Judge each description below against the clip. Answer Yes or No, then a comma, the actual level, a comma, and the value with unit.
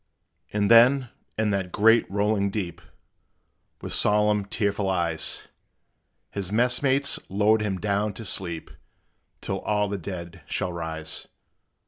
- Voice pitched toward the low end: Yes, low, 100 Hz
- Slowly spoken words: Yes, slow, 125 wpm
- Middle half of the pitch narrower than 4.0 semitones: Yes, narrow, 2.6 semitones